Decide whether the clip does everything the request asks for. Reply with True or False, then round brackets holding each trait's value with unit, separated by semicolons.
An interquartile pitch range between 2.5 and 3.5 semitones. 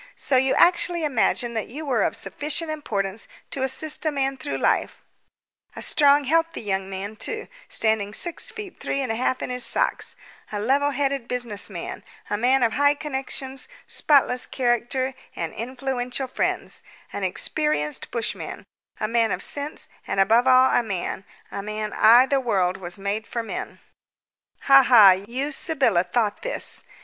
False (4.7 semitones)